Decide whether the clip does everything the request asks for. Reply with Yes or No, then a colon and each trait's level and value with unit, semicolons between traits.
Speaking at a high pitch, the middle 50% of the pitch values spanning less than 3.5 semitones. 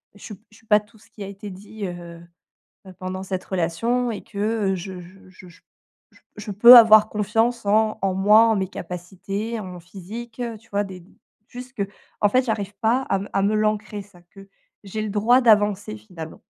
Yes: high, 205 Hz; narrow, 2.6 semitones